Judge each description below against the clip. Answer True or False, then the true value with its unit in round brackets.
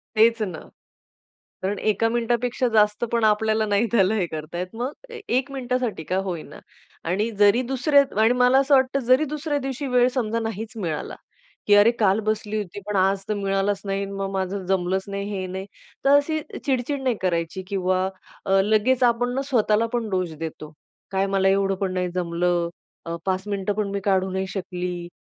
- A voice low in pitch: False (205 Hz)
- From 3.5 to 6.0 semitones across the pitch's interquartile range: True (4.0 semitones)